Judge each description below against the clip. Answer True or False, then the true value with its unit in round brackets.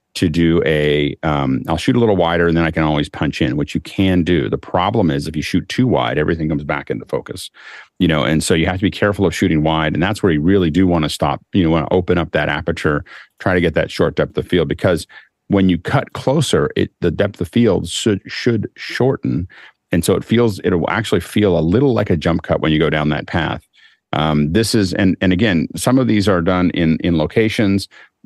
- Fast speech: True (245 wpm)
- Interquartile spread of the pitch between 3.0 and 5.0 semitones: True (3.8 semitones)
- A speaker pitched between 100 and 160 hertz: False (85 Hz)